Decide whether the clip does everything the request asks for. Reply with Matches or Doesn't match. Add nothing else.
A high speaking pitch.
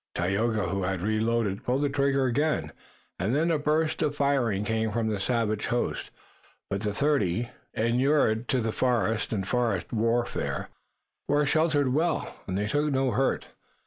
Doesn't match